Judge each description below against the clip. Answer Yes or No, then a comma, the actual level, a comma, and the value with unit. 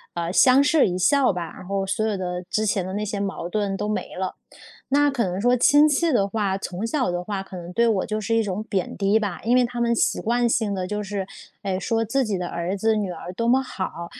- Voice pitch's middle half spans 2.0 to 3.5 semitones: No, average, 3.9 semitones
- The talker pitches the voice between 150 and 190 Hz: No, high, 210 Hz